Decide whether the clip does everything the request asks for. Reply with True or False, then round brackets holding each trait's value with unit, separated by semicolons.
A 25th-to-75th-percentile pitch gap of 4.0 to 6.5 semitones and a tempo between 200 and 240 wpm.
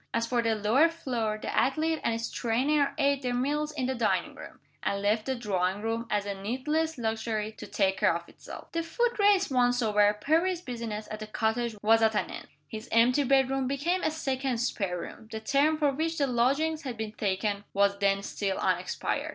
True (4.8 semitones; 205 wpm)